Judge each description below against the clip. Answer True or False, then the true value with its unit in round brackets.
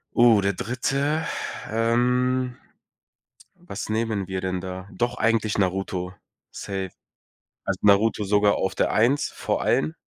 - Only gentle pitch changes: False (4.0 semitones)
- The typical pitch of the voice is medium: False (105 Hz)